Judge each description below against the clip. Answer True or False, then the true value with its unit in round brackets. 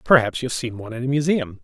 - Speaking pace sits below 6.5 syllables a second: False (7.2 syllables/s)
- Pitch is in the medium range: False (130 Hz)